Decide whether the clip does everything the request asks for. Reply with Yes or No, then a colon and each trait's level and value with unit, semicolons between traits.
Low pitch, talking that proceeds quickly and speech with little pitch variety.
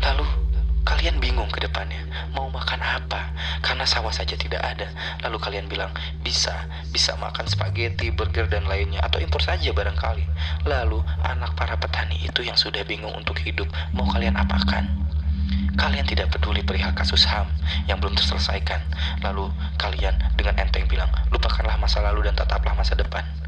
Yes: very low, 75 Hz; fast, 150 wpm; narrow, 1.5 semitones